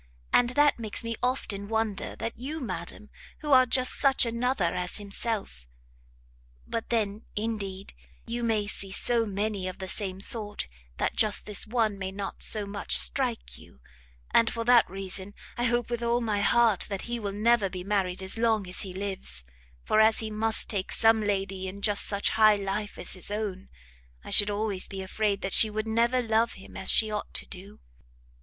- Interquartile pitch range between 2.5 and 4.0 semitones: Yes, average, 2.8 semitones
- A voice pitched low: No, high, 210 Hz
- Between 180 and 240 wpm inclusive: Yes, average, 190 wpm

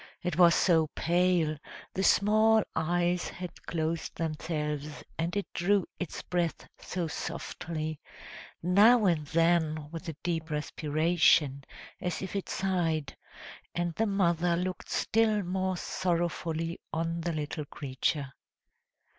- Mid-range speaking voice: Yes, medium, 170 Hz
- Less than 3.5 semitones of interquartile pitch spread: Yes, narrow, 2.4 semitones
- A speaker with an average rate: No, slow, 120 wpm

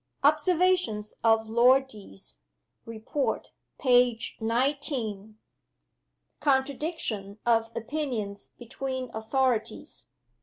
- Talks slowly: Yes, slow, 70 wpm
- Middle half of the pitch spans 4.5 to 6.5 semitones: No, average, 3.7 semitones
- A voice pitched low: No, high, 240 Hz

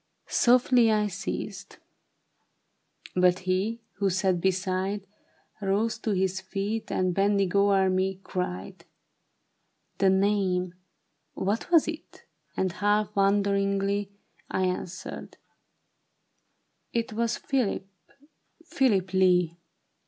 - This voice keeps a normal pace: No, slow, 110 wpm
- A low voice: No, high, 195 Hz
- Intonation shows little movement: Yes, narrow, 2.0 semitones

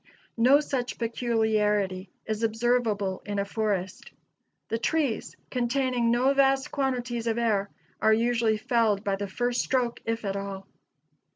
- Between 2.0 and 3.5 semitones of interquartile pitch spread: Yes, average, 3.0 semitones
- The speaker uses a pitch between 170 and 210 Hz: No, high, 230 Hz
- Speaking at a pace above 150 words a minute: No, slow, 135 wpm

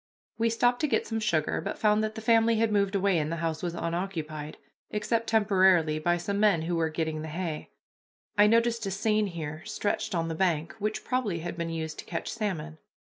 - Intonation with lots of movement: No, average, 4.9 semitones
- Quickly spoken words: Yes, fast, 210 wpm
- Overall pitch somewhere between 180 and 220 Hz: Yes, medium, 185 Hz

